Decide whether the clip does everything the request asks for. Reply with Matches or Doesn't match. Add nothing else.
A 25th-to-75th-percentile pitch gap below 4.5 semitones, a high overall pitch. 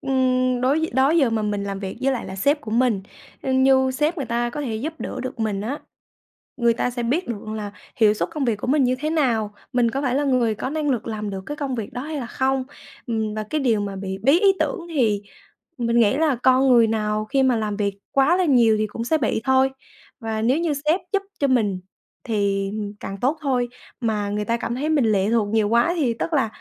Matches